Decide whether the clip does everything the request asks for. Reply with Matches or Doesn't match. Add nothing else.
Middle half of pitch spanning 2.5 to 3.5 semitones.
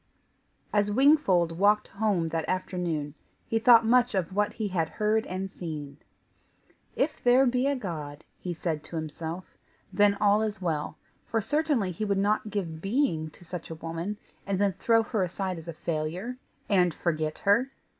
Doesn't match